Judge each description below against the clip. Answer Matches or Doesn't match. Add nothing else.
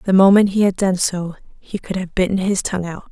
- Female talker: Matches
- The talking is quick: Matches